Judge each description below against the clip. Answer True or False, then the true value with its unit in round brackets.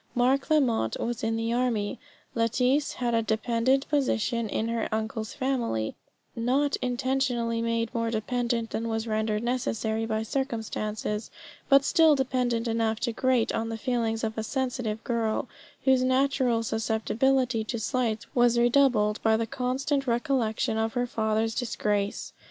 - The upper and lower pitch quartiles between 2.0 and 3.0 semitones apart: True (2.5 semitones)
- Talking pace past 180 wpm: False (145 wpm)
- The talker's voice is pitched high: True (230 Hz)